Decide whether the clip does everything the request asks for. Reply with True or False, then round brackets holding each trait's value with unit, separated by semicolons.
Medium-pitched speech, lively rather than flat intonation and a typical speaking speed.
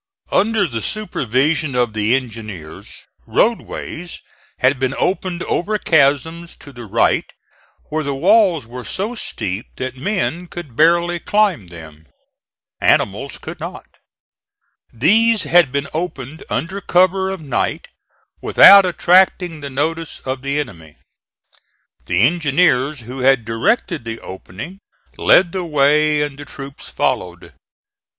False (150 Hz; 5.9 semitones; 125 wpm)